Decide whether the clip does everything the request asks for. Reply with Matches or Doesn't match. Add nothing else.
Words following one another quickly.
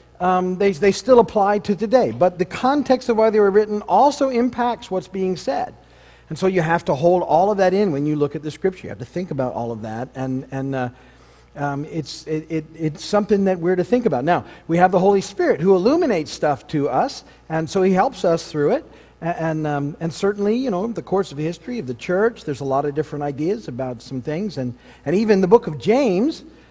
Matches